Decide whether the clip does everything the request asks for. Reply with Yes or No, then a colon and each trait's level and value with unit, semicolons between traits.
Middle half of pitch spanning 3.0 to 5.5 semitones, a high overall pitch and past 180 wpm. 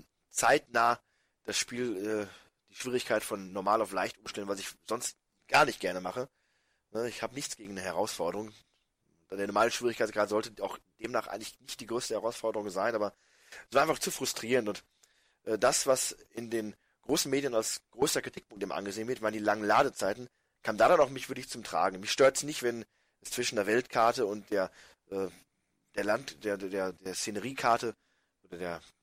No: average, 3.3 semitones; low, 110 Hz; fast, 190 wpm